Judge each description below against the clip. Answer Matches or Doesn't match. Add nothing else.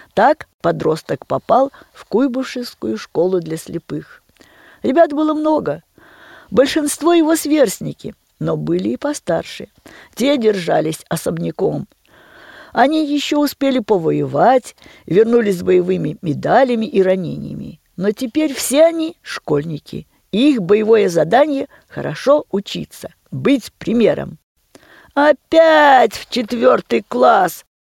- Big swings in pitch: Matches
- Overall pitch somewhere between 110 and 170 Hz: Doesn't match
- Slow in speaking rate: Matches